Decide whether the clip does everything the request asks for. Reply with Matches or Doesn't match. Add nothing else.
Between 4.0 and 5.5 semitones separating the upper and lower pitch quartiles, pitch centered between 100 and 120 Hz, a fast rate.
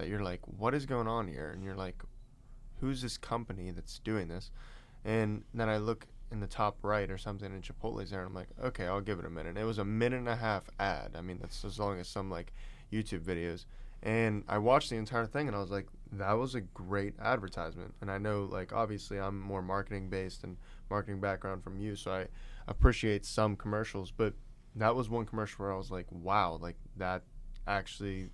Doesn't match